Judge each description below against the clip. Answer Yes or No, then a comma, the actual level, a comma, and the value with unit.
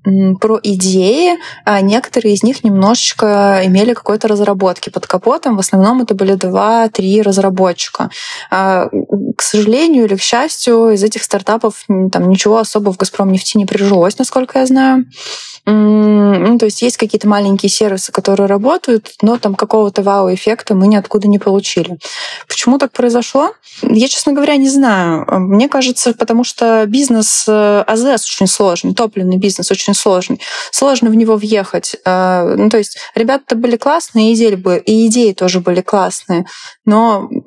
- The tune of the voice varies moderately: Yes, average, 3.3 semitones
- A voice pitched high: Yes, high, 215 Hz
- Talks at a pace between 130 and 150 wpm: Yes, average, 140 wpm